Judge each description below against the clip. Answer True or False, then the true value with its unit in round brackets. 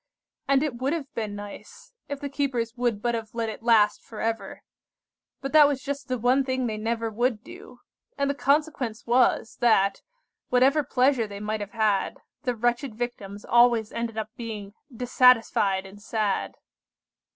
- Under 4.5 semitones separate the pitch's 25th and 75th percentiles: True (3.3 semitones)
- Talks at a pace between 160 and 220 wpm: True (170 wpm)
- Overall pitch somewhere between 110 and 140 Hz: False (235 Hz)